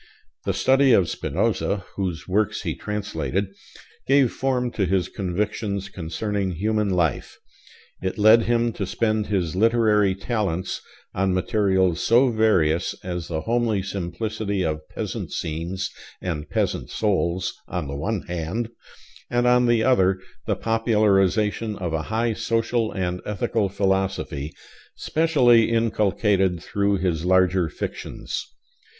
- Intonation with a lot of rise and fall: No, average, 3.5 semitones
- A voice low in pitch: Yes, low, 100 Hz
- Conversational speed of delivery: No, slow, 125 wpm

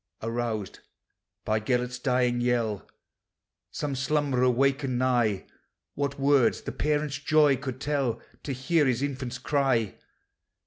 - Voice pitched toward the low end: Yes, low, 130 Hz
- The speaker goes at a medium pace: No, slow, 120 wpm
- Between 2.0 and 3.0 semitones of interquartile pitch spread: Yes, narrow, 2.6 semitones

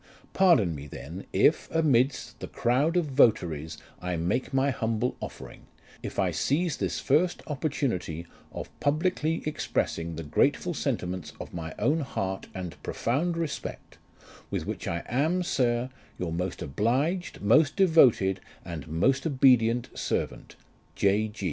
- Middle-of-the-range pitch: No, low, 120 Hz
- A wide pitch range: Yes, wide, 8.8 semitones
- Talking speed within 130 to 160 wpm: Yes, average, 140 wpm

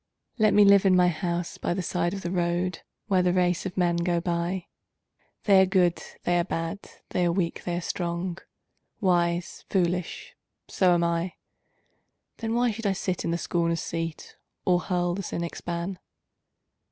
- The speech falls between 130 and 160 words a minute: No, average, 175 wpm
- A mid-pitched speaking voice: Yes, medium, 175 Hz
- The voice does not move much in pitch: Yes, narrow, 1.6 semitones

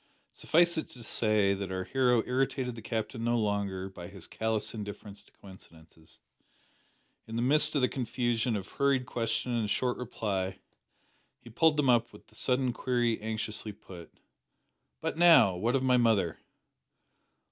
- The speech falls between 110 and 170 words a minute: Yes, average, 160 wpm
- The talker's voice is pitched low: Yes, low, 115 Hz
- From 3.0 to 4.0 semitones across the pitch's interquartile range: Yes, average, 3.7 semitones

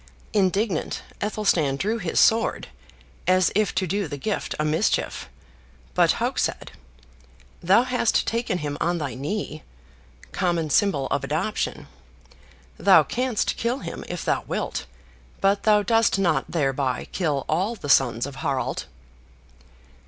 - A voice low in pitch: No, medium, 180 Hz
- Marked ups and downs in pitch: Yes, wide, 6.2 semitones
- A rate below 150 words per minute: Yes, slow, 135 wpm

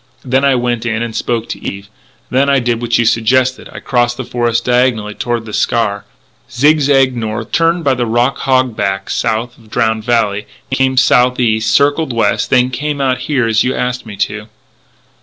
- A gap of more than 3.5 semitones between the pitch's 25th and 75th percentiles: No, narrow, 2.5 semitones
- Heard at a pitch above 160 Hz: No, low, 120 Hz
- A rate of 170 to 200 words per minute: Yes, average, 190 wpm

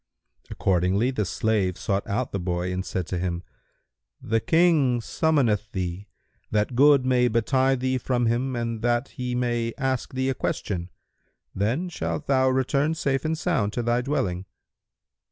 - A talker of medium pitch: No, low, 120 Hz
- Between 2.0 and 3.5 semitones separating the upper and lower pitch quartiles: No, average, 4.6 semitones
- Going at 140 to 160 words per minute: Yes, average, 155 wpm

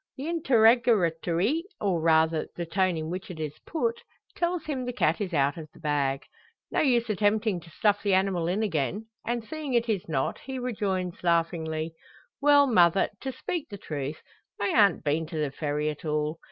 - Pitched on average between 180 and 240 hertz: Yes, medium, 185 Hz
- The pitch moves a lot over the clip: Yes, wide, 6.8 semitones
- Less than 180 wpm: No, average, 185 wpm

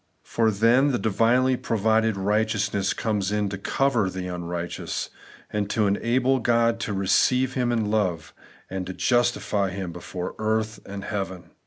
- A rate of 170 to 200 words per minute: No, average, 145 wpm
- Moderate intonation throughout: Yes, average, 3.3 semitones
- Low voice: Yes, low, 105 Hz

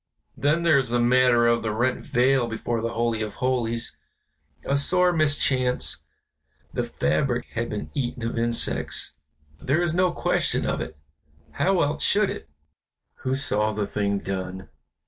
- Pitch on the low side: Yes, low, 120 Hz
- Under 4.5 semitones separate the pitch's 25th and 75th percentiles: Yes, average, 3.7 semitones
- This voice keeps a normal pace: Yes, average, 160 wpm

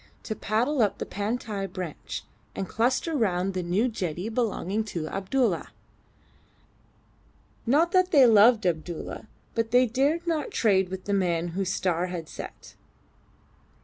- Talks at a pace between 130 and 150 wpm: Yes, average, 140 wpm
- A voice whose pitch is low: No, high, 205 Hz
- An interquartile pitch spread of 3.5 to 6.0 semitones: Yes, average, 5.1 semitones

